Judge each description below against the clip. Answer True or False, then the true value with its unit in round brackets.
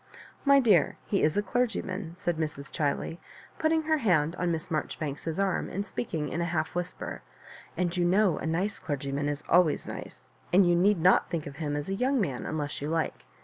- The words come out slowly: False (205 wpm)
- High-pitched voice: False (175 Hz)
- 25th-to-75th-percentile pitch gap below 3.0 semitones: False (4.3 semitones)